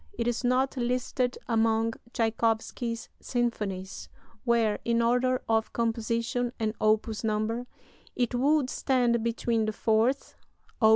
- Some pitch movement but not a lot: No, narrow, 1.8 semitones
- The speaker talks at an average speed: No, slow, 120 wpm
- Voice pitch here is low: No, high, 230 Hz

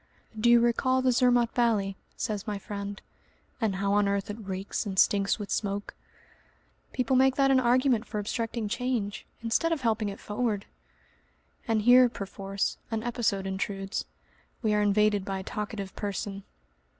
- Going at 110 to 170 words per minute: Yes, average, 160 wpm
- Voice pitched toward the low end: No, high, 210 Hz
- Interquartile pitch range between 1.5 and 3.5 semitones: Yes, average, 3.1 semitones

